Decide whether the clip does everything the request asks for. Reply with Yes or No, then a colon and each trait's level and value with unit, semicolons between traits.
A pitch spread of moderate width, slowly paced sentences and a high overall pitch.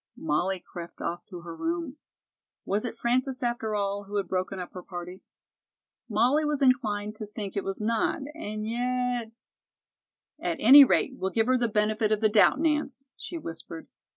No: average, 4.4 semitones; average, 175 wpm; high, 215 Hz